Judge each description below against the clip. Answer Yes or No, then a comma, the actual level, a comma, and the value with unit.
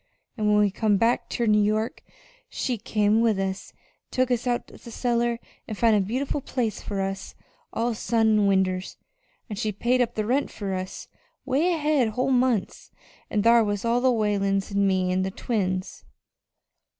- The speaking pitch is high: Yes, high, 215 Hz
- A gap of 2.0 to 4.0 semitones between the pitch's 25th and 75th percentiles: Yes, average, 3.3 semitones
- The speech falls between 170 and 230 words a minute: Yes, average, 185 wpm